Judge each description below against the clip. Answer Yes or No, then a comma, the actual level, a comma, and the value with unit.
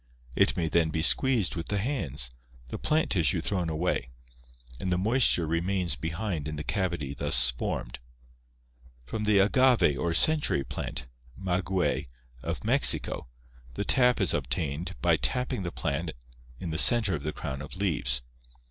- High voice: No, very low, 85 Hz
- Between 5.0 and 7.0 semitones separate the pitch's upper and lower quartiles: Yes, average, 5.3 semitones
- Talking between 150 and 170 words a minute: Yes, average, 155 wpm